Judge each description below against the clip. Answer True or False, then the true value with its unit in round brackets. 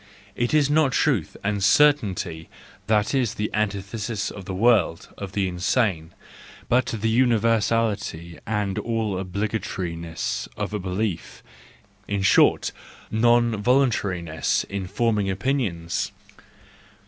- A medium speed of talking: False (110 wpm)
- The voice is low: True (105 Hz)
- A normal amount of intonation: True (3.7 semitones)